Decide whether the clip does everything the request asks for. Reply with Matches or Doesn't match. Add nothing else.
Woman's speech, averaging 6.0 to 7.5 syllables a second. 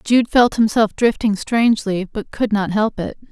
Doesn't match